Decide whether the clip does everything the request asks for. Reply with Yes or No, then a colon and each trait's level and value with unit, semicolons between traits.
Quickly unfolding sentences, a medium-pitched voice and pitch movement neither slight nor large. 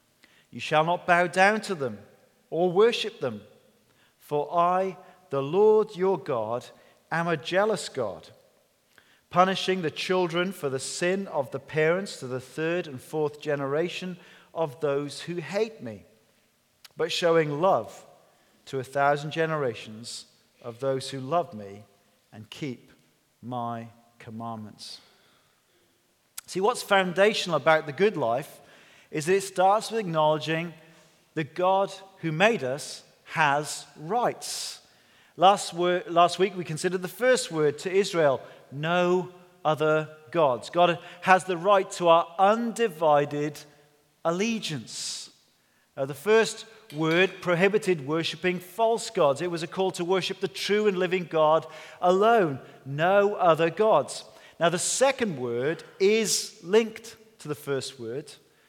No: slow, 135 wpm; medium, 170 Hz; average, 4.7 semitones